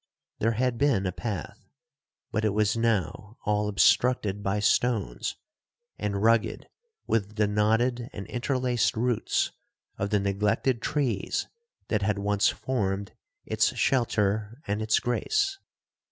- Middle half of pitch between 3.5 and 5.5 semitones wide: No, average, 3.0 semitones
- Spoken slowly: Yes, slow, 125 wpm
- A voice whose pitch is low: Yes, low, 110 Hz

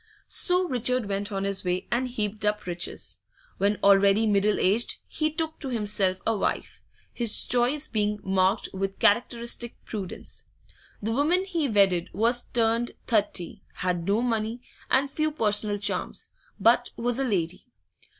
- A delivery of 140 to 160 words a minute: Yes, average, 150 wpm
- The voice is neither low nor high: No, high, 215 Hz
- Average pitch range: Yes, average, 3.7 semitones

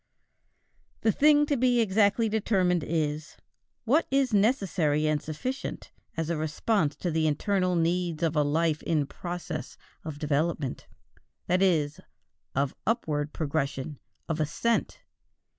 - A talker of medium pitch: Yes, medium, 165 Hz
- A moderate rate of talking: No, slow, 125 wpm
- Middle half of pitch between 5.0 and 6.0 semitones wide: Yes, wide, 5.4 semitones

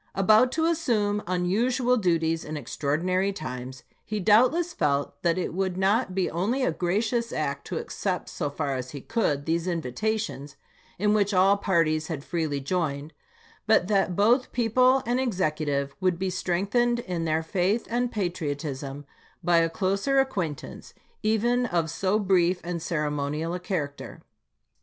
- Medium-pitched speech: Yes, medium, 180 Hz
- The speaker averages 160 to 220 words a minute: No, average, 150 wpm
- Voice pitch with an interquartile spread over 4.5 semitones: Yes, wide, 5.6 semitones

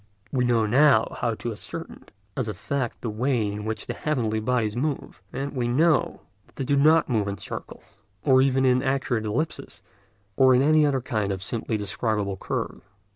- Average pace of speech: Yes, average, 185 wpm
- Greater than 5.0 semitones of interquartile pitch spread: No, average, 3.9 semitones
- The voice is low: Yes, low, 125 Hz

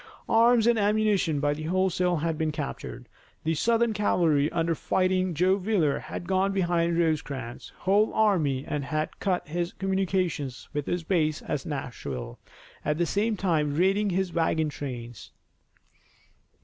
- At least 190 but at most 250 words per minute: No, average, 145 wpm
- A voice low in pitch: No, medium, 170 Hz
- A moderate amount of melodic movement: Yes, average, 4.3 semitones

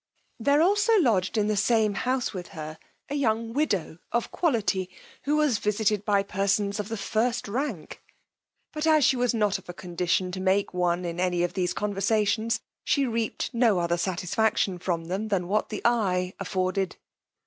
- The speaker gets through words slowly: No, average, 175 wpm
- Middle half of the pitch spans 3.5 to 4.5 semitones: Yes, average, 4.2 semitones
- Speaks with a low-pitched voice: No, high, 205 Hz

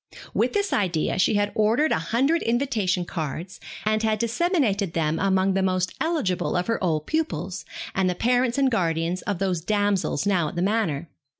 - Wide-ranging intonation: No, average, 4.5 semitones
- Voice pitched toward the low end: No, high, 195 Hz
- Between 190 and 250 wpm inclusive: No, average, 180 wpm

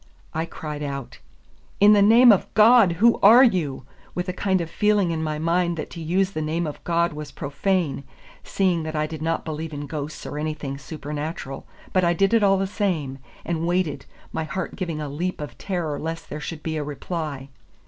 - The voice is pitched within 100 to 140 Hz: No, medium, 165 Hz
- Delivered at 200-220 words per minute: Yes, fast, 205 wpm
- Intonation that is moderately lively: Yes, average, 3.7 semitones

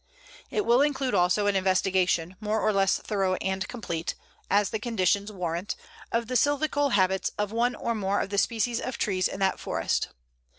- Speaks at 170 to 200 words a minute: Yes, average, 180 wpm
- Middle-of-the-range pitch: No, high, 205 Hz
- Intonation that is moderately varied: Yes, average, 3.7 semitones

